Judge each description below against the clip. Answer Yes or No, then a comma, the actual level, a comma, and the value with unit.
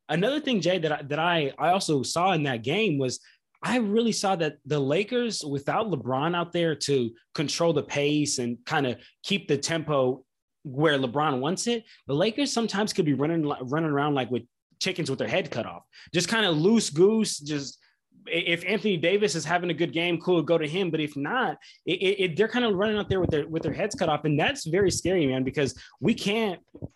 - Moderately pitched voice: Yes, medium, 165 Hz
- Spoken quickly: Yes, fast, 220 wpm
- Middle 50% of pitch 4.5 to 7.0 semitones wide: Yes, average, 5.3 semitones